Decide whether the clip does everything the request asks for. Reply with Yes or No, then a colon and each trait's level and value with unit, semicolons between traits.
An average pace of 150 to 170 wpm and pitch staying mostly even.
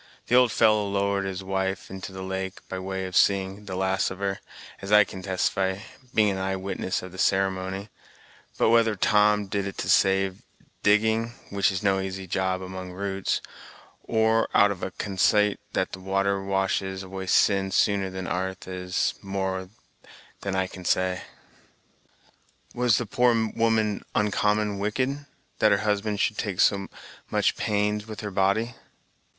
Yes: average, 160 wpm; narrow, 1.7 semitones